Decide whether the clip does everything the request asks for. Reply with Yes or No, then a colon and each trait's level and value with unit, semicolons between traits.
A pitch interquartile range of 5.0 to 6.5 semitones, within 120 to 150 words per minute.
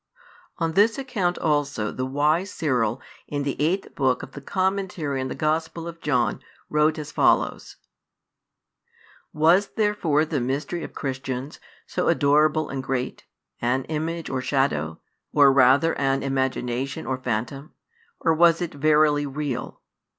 No: average, 3.5 semitones; average, 140 wpm